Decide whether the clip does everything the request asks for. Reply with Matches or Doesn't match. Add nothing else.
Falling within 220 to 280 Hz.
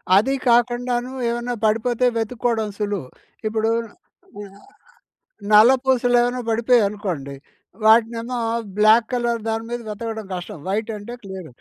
Matches